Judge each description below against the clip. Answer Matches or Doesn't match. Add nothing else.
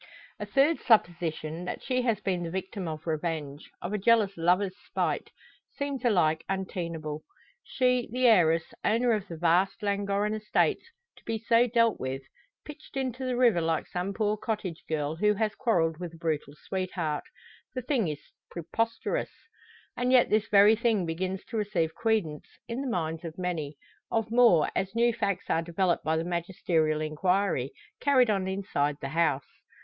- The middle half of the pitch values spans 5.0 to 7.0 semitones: Matches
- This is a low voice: Doesn't match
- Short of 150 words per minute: Doesn't match